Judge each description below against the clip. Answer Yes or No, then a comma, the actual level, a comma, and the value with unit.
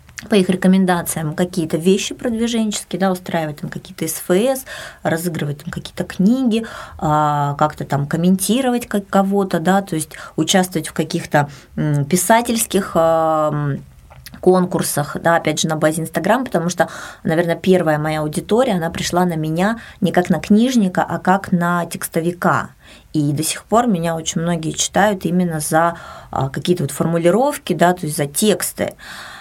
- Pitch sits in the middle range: Yes, medium, 175 Hz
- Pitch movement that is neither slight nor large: Yes, average, 3.5 semitones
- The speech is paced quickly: No, average, 140 wpm